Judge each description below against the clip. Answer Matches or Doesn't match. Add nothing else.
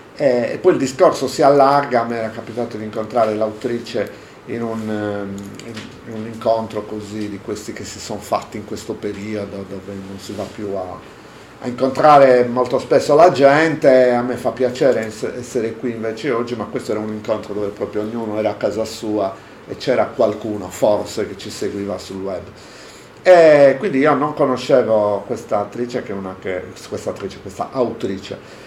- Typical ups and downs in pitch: Matches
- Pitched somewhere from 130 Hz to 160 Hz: Doesn't match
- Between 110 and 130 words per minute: Doesn't match